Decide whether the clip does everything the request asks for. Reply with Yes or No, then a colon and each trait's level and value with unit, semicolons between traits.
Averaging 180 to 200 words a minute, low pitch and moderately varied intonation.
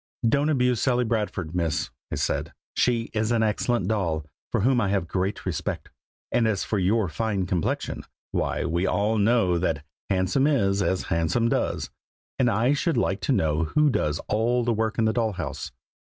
Yes: average, 185 wpm; low, 110 Hz; average, 4.5 semitones